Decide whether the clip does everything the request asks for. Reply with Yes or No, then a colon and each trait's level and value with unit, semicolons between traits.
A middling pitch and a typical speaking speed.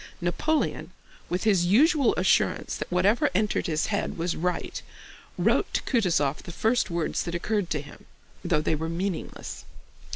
Yes: medium, 180 Hz; average, 155 wpm